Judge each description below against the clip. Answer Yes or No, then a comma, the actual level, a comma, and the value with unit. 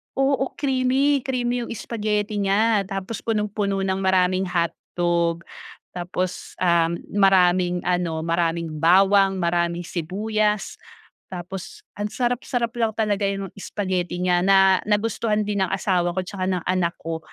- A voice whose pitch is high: Yes, high, 195 Hz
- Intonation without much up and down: No, average, 3.2 semitones